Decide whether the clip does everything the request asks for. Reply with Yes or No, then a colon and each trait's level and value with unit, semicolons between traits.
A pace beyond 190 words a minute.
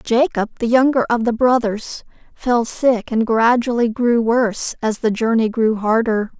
No: average, 160 wpm